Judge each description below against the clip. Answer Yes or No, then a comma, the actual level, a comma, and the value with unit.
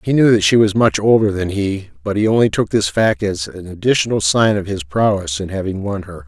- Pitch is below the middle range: Yes, low, 105 Hz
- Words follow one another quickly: Yes, fast, 250 wpm